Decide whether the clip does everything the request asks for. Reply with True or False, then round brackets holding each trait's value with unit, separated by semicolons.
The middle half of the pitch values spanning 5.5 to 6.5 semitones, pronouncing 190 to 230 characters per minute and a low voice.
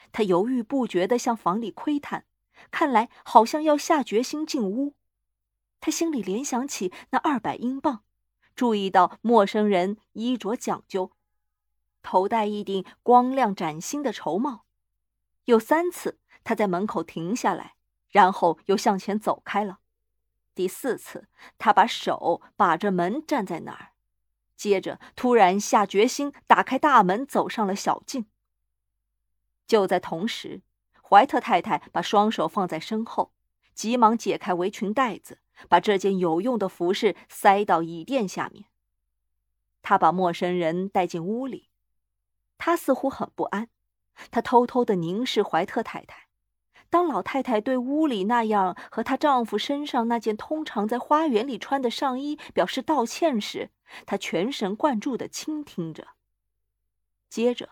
False (5.9 semitones; 215 characters per minute; 215 Hz)